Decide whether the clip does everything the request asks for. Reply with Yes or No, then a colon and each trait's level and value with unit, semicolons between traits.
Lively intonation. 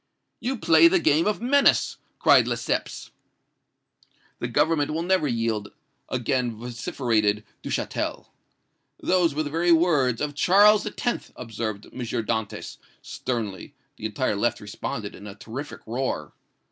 Yes: wide, 7.0 semitones